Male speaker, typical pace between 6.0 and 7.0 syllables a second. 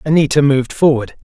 Yes: male; 6.4 syllables/s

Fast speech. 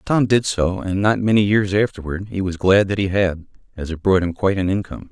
Yes: fast, 245 wpm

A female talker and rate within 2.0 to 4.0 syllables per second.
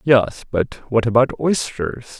No: male; 3.7 syllables/s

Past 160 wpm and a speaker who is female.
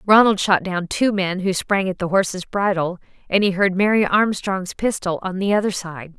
Yes: fast, 205 wpm; female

